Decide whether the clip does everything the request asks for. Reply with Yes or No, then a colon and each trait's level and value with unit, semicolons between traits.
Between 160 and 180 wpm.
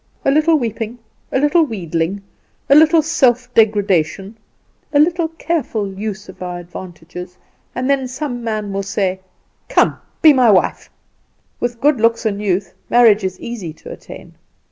No: average, 150 wpm